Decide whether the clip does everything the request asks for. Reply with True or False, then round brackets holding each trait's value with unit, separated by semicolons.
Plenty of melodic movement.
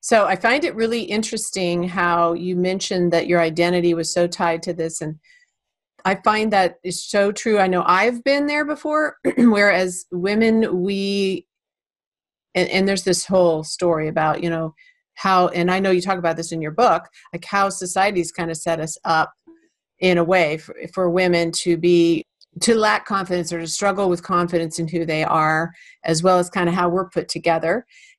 False (2.8 semitones)